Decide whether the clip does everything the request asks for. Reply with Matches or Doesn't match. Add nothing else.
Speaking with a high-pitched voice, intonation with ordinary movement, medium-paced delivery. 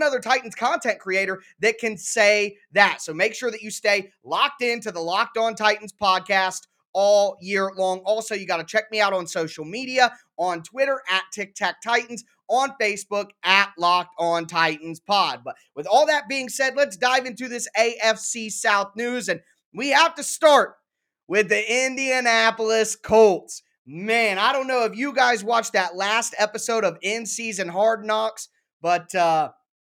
Matches